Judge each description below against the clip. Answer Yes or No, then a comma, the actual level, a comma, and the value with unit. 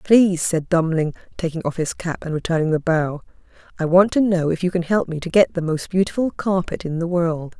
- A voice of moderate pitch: Yes, medium, 170 Hz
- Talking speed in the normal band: No, fast, 230 wpm